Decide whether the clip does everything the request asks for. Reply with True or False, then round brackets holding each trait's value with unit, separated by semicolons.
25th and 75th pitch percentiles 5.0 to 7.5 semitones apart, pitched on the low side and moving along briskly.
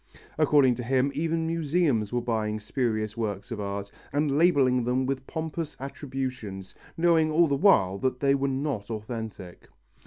False (5.4 semitones; 130 Hz; 155 wpm)